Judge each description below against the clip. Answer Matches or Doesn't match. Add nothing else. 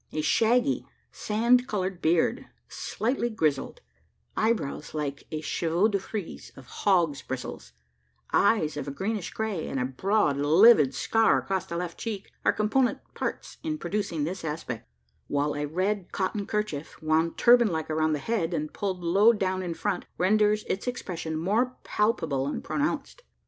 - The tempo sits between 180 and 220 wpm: Doesn't match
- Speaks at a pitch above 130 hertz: Matches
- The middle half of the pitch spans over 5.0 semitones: Matches